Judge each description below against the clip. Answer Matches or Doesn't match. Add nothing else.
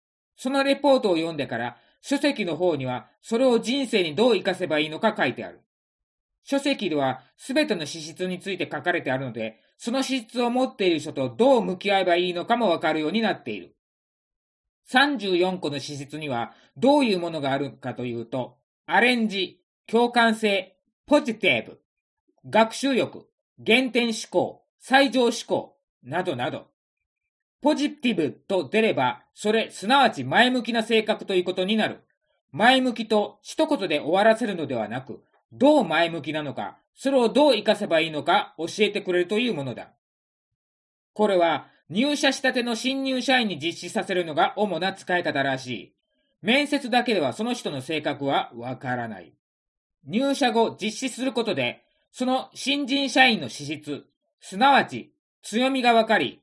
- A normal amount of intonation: Doesn't match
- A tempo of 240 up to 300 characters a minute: Doesn't match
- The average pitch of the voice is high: Matches